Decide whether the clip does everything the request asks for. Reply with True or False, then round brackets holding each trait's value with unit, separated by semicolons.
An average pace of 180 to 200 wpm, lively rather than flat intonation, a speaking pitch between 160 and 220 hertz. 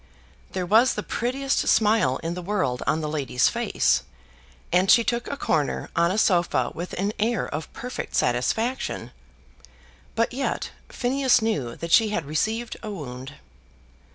False (155 wpm; 7.3 semitones; 190 Hz)